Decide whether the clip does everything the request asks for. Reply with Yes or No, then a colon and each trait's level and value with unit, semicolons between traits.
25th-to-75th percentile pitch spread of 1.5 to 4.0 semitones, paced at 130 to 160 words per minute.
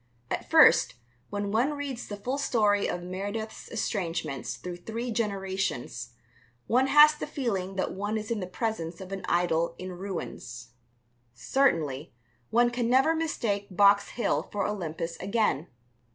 No: average, 4.8 semitones; average, 145 wpm